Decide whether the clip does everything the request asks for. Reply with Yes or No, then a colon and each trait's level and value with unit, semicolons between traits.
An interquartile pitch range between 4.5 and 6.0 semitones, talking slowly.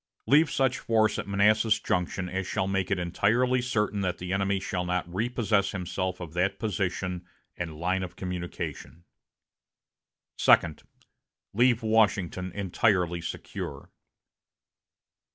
No: average, 3.2 semitones; slow, 120 wpm